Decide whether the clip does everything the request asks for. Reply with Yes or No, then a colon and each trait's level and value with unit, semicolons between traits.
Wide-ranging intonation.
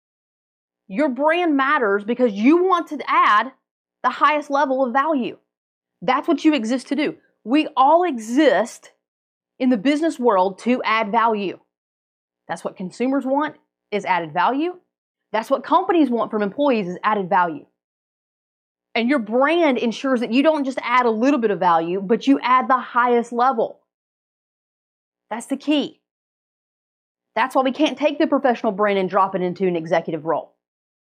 Yes: wide, 7.5 semitones